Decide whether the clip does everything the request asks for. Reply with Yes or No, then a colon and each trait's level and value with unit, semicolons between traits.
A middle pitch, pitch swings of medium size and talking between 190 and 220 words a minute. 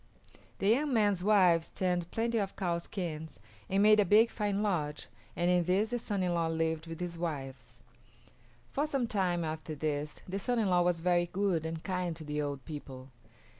Yes: medium, 175 Hz; average, 4.0 semitones; average, 195 wpm